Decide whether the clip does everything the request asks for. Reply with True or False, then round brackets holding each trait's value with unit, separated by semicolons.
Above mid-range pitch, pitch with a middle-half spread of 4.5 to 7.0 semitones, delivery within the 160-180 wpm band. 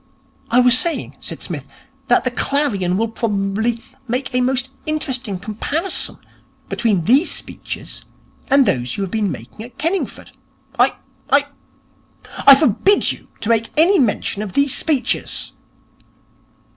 False (245 Hz; 5.3 semitones; 135 wpm)